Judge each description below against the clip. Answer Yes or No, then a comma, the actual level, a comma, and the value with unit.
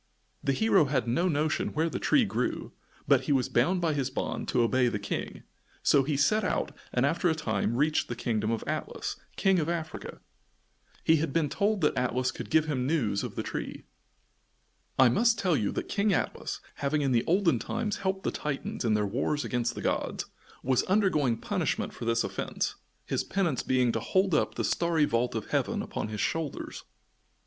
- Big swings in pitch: Yes, wide, 5.7 semitones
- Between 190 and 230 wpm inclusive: Yes, average, 195 wpm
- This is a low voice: No, medium, 145 Hz